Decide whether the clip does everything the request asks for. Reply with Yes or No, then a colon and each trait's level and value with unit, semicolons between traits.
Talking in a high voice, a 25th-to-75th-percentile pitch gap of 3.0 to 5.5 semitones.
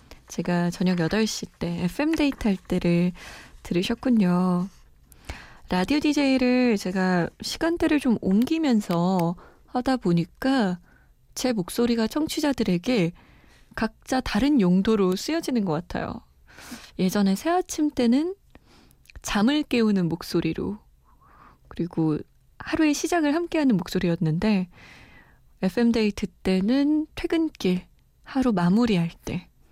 No: high, 215 Hz; wide, 6.8 semitones